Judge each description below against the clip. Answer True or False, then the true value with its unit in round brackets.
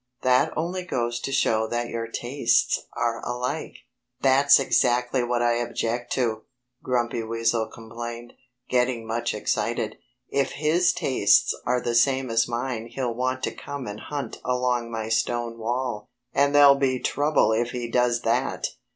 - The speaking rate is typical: True (150 wpm)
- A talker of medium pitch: False (120 Hz)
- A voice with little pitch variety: True (2.1 semitones)